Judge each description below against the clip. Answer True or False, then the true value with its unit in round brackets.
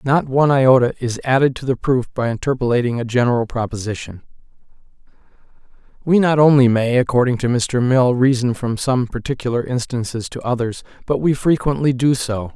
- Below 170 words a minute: True (160 wpm)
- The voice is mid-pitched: False (125 Hz)